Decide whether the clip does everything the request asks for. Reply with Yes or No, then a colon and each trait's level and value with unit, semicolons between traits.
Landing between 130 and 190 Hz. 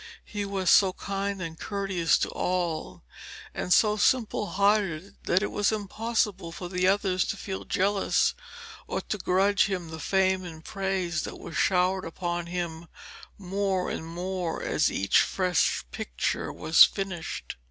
Yes: medium, 185 Hz